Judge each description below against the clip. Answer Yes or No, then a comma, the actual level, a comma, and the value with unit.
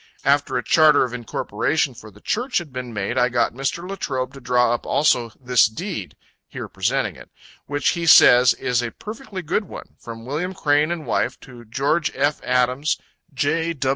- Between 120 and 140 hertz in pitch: Yes, low, 135 Hz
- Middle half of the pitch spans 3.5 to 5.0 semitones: Yes, average, 4.6 semitones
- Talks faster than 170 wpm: Yes, average, 180 wpm